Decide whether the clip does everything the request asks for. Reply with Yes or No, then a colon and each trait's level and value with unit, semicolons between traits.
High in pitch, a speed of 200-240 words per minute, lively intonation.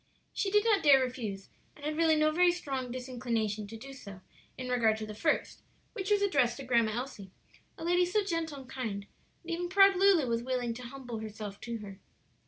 Yes: very high, 255 Hz; fast, 205 wpm; wide, 6.7 semitones